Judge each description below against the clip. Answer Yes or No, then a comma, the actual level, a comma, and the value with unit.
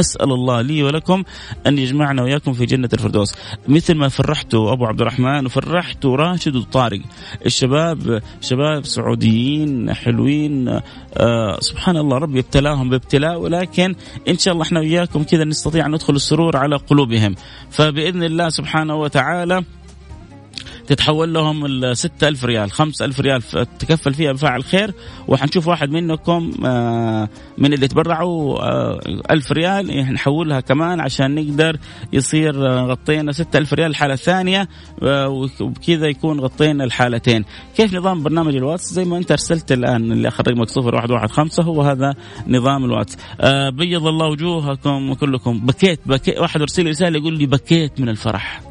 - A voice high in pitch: No, medium, 140 Hz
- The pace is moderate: No, fast, 140 wpm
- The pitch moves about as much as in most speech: Yes, average, 3.9 semitones